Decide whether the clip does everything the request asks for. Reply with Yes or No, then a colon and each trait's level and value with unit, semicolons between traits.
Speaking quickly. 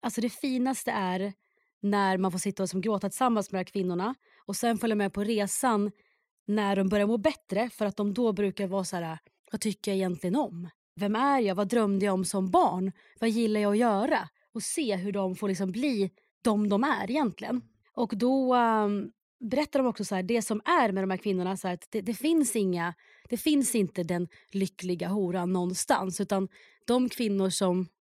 Yes: fast, 210 wpm